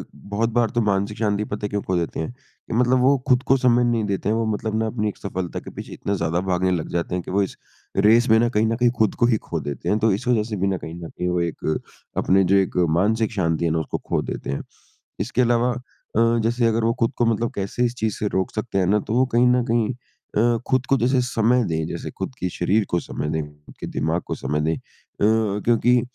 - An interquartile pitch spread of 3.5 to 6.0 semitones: Yes, average, 4.2 semitones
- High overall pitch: No, low, 110 Hz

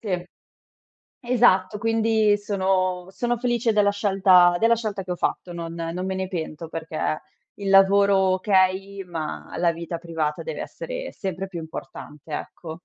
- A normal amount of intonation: Yes, average, 3.3 semitones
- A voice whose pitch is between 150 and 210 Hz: Yes, high, 190 Hz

